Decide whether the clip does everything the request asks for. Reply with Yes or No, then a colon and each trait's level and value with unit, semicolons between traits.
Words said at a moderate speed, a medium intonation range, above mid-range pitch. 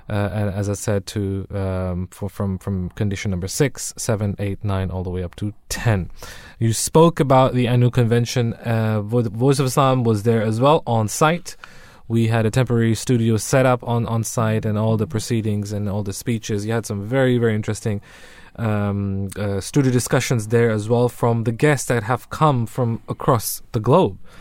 No: average, 190 wpm; average, 3.2 semitones; low, 115 Hz